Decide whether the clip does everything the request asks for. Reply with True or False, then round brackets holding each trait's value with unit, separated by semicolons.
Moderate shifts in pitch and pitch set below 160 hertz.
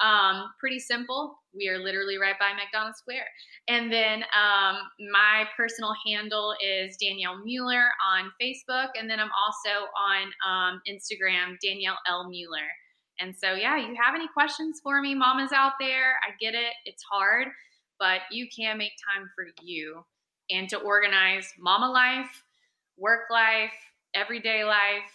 False (3.7 semitones; 210 Hz)